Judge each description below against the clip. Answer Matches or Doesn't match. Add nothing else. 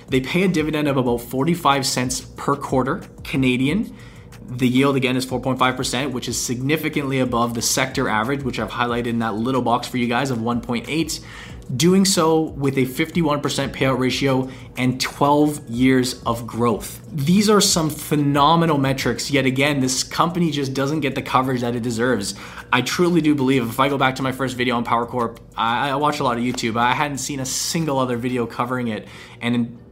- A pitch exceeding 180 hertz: Doesn't match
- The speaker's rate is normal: Matches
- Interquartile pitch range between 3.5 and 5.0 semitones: Doesn't match